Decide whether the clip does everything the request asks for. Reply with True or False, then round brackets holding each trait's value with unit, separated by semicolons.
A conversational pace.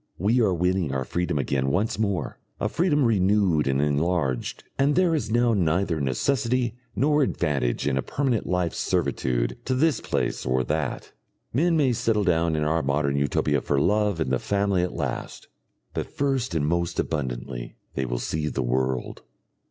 True (170 wpm)